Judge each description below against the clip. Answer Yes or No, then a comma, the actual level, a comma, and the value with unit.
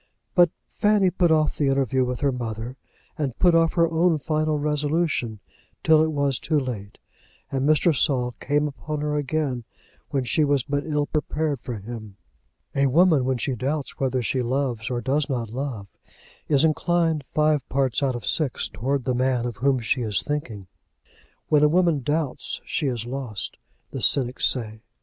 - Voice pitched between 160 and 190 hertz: No, medium, 140 Hz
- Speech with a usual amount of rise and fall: Yes, average, 3.6 semitones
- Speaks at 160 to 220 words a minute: Yes, average, 175 wpm